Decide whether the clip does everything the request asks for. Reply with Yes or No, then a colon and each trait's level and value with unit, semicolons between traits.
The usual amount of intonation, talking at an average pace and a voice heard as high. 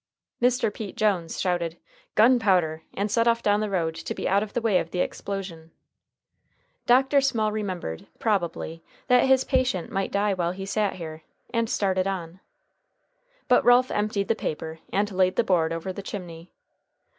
Yes: average, 3.9 semitones; average, 170 wpm; high, 195 Hz